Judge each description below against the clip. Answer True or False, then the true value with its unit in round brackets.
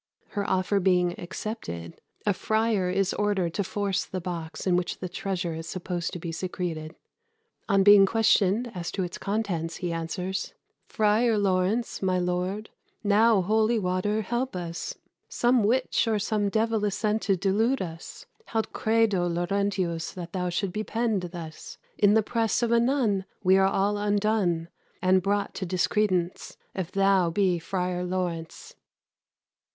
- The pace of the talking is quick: False (155 wpm)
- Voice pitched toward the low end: False (195 Hz)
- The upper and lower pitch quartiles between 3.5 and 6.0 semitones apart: False (3.1 semitones)